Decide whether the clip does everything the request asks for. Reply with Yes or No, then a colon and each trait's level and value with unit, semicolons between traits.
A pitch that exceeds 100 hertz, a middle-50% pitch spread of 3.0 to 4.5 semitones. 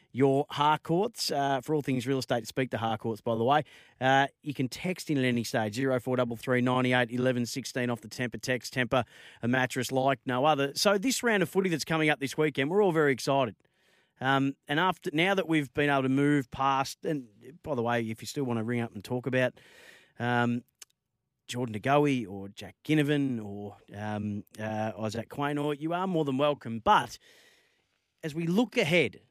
Yes: low, 135 Hz; average, 4.1 semitones